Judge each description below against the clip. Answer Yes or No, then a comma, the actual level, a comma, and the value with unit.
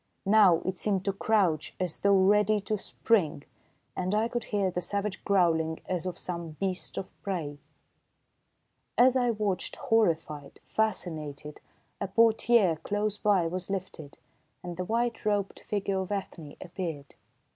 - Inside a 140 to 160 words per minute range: Yes, average, 145 wpm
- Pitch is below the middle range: No, high, 190 Hz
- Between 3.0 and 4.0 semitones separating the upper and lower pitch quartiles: Yes, average, 3.6 semitones